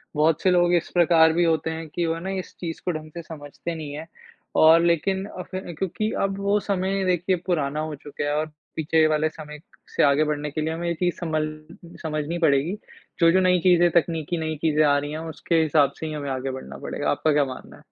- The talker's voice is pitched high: No, medium, 160 Hz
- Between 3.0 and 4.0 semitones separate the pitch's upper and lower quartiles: No, narrow, 2.5 semitones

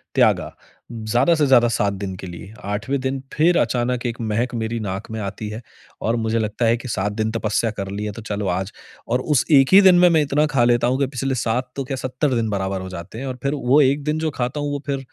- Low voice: Yes, low, 120 Hz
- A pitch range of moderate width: Yes, average, 4.2 semitones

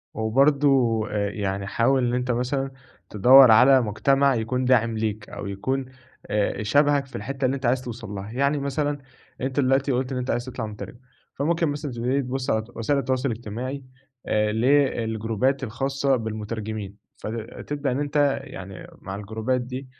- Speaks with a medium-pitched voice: No, low, 125 Hz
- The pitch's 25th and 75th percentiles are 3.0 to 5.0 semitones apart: Yes, average, 3.7 semitones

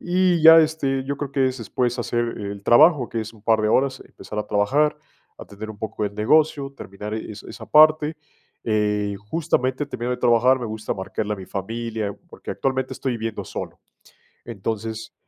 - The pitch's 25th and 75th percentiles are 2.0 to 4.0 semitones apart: No, average, 4.4 semitones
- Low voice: Yes, low, 120 Hz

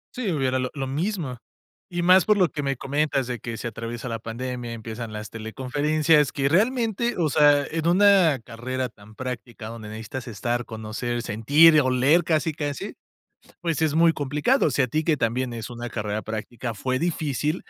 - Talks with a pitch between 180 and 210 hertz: No, low, 130 Hz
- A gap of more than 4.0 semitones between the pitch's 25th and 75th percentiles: Yes, average, 5.1 semitones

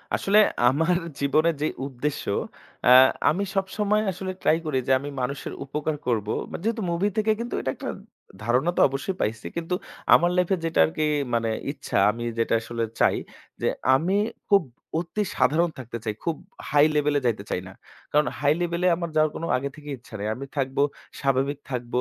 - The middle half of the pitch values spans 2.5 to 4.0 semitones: No, average, 5.2 semitones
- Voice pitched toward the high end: No, medium, 150 Hz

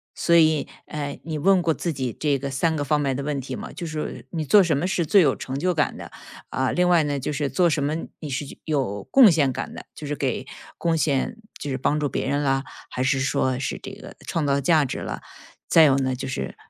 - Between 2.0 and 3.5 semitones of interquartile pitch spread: Yes, average, 3.1 semitones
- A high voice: No, medium, 145 Hz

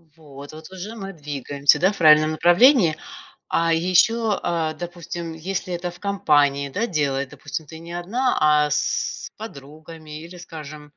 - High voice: No, medium, 160 Hz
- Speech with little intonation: No, average, 3.3 semitones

